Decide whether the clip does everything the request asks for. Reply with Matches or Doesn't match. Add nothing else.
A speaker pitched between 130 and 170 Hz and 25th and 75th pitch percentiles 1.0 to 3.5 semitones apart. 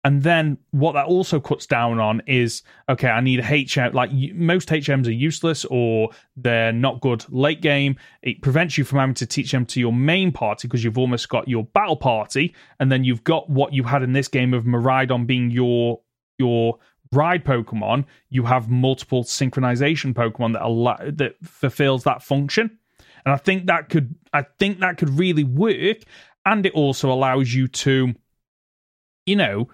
Matches